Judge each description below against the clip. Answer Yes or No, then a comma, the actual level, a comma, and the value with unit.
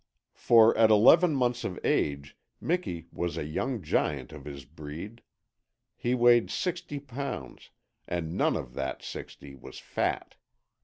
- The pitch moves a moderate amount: No, wide, 8.7 semitones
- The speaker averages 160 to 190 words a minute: No, average, 140 wpm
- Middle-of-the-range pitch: No, low, 105 Hz